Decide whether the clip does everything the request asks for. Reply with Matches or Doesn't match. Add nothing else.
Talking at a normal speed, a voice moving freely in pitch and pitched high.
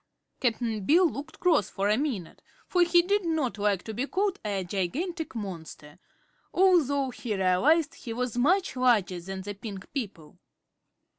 Matches